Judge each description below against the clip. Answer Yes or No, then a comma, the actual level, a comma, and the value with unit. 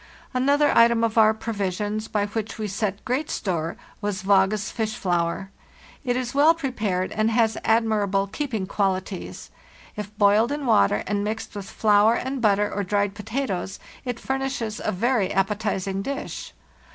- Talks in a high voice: Yes, high, 215 Hz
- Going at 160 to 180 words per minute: No, average, 150 wpm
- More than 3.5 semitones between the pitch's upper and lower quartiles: No, average, 3.1 semitones